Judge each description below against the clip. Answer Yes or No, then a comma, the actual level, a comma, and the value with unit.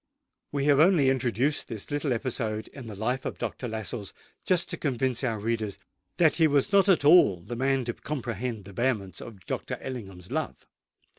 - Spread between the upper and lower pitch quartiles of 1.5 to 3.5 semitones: No, average, 4.4 semitones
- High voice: No, low, 125 Hz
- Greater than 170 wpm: Yes, average, 180 wpm